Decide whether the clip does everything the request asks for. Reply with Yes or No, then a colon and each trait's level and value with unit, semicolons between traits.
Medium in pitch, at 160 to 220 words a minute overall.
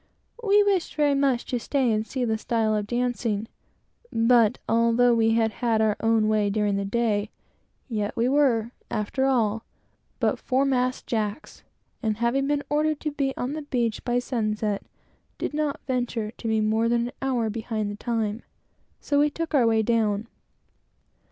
No: high, 235 Hz; average, 170 wpm